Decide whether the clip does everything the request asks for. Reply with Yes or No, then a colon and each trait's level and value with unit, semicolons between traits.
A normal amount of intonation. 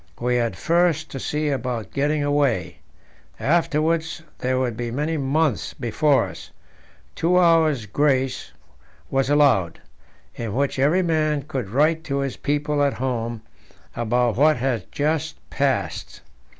Yes: average, 3.7 semitones